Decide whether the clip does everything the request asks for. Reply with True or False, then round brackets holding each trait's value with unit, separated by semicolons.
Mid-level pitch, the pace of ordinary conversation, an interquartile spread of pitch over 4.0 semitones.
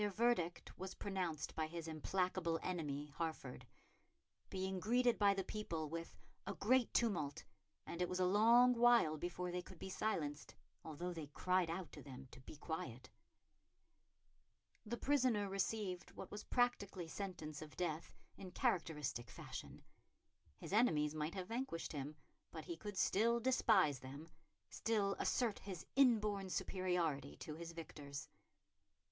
True (180 Hz; 145 wpm; 4.9 semitones)